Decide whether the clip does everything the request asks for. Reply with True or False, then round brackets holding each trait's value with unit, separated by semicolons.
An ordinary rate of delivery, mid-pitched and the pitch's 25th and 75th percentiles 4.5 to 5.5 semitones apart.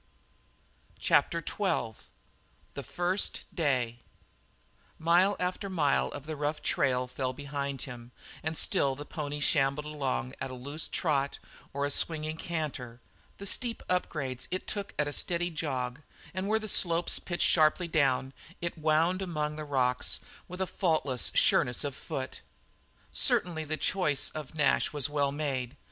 False (150 wpm; 150 Hz; 3.9 semitones)